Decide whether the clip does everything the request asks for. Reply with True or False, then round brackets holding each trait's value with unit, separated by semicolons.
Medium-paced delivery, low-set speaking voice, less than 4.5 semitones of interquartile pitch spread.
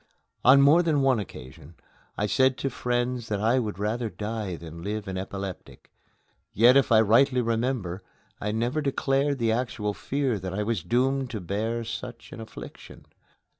True (170 wpm; 115 Hz; 3.8 semitones)